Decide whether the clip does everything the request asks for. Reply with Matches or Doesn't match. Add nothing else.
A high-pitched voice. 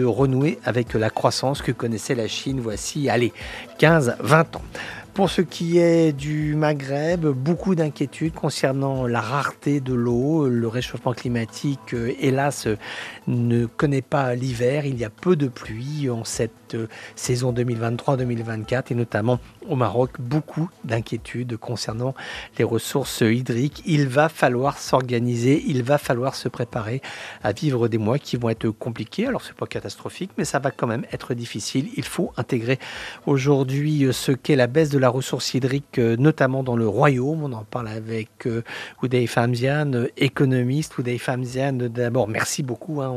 Doesn't match